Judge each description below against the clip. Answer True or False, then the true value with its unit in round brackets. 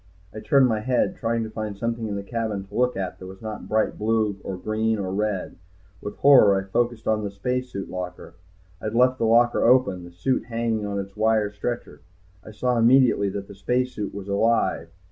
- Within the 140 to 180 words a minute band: False (205 wpm)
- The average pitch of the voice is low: True (110 Hz)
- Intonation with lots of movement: False (2.9 semitones)